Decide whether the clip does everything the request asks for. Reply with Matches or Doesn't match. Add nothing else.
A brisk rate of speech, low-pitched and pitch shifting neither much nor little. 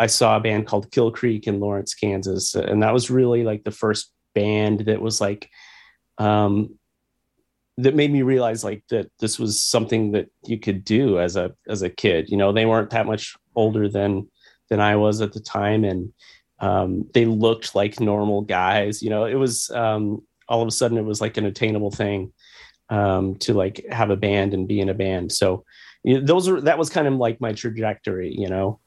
Doesn't match